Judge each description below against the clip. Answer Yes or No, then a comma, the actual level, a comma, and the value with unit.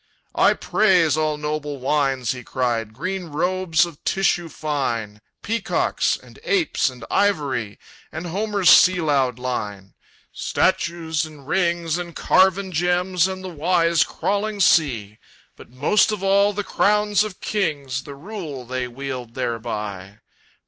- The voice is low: No, medium, 155 Hz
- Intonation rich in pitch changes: Yes, wide, 6.5 semitones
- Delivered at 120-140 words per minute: Yes, slow, 135 wpm